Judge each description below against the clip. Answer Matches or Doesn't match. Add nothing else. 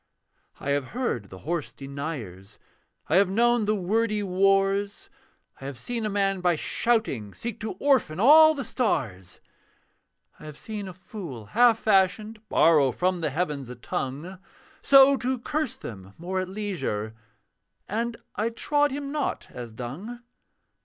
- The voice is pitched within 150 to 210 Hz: Matches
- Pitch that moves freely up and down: Matches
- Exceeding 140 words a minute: Matches